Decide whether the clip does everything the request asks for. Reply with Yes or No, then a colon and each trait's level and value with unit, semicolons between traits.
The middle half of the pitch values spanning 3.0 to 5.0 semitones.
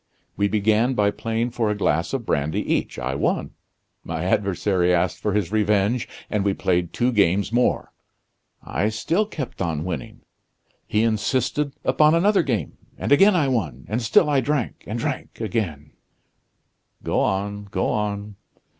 Yes: average, 4.5 semitones